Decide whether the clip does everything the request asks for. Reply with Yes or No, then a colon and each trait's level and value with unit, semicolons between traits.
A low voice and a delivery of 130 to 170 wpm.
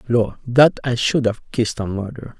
No: low, 120 Hz; average, 200 wpm